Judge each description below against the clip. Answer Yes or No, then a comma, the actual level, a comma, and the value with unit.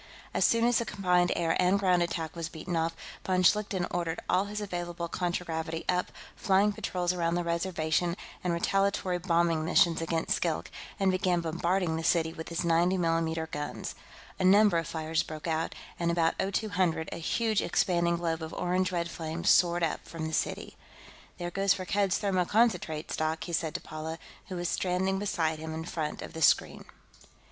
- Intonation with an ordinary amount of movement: No, narrow, 2.3 semitones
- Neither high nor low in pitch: Yes, medium, 175 Hz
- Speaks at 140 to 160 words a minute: No, average, 180 wpm